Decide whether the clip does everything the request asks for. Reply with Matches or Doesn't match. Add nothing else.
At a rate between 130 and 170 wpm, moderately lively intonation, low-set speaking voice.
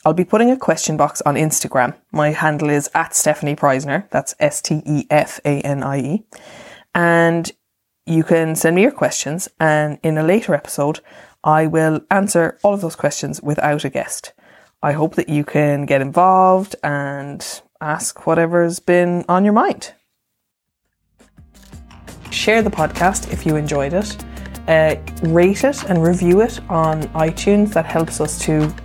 Doesn't match